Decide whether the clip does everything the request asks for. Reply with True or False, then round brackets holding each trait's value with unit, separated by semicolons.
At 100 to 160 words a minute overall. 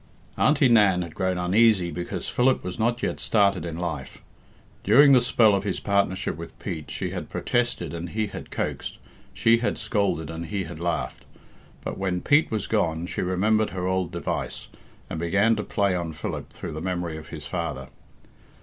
False (185 wpm)